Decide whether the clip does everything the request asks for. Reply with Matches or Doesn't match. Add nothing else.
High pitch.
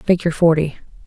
Doesn't match